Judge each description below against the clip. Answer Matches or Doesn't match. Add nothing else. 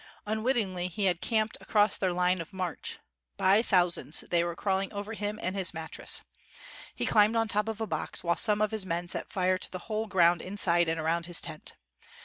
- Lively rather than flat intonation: Doesn't match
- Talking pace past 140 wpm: Matches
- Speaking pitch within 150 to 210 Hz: Matches